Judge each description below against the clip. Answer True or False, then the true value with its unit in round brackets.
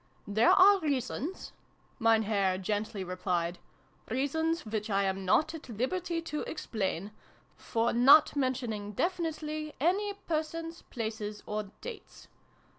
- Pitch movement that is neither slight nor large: False (7.5 semitones)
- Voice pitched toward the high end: True (245 Hz)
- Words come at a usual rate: False (120 wpm)